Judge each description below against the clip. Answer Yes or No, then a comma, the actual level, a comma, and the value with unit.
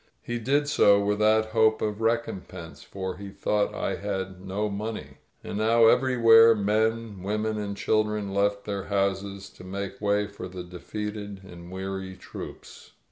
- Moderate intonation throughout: No, narrow, 2.0 semitones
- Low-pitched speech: Yes, low, 105 Hz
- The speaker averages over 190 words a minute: No, average, 155 wpm